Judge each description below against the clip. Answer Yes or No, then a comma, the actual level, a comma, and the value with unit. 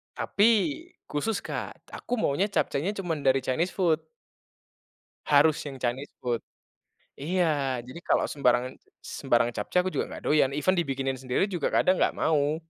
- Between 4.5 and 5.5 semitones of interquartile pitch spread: Yes, average, 5.2 semitones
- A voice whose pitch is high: No, medium, 145 Hz